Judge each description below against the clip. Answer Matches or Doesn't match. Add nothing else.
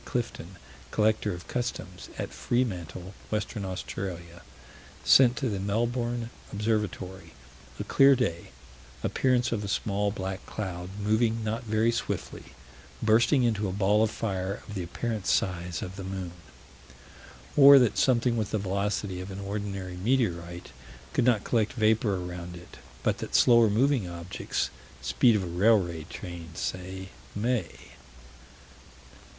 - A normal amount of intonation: Matches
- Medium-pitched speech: Doesn't match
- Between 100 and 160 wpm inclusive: Matches